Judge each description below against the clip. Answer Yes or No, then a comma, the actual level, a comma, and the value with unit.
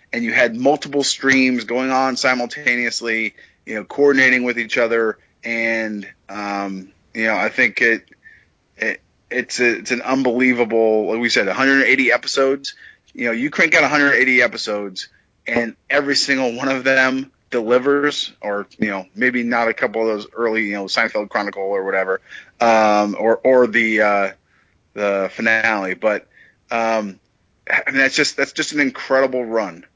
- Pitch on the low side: Yes, low, 120 Hz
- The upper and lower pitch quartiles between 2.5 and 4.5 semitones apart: Yes, average, 3.6 semitones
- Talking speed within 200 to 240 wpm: No, average, 160 wpm